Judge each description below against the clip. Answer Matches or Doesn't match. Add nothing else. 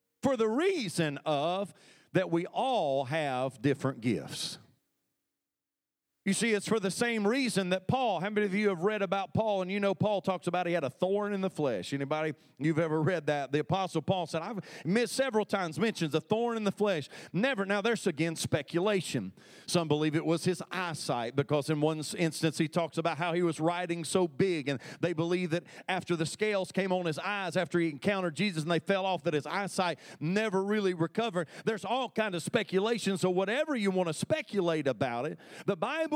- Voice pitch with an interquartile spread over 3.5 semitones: Matches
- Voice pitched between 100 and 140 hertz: Doesn't match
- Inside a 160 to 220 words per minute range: Matches